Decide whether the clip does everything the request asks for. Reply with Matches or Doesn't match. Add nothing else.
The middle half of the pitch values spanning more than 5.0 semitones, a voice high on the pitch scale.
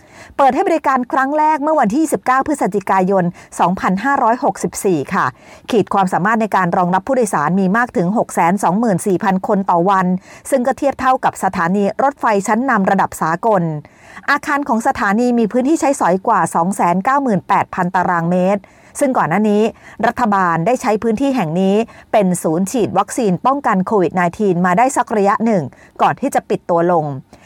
Matches